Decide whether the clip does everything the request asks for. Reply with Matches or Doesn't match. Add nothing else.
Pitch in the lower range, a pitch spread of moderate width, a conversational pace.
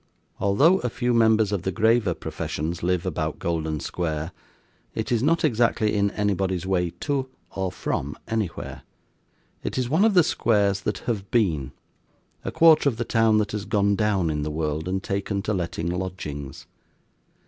Matches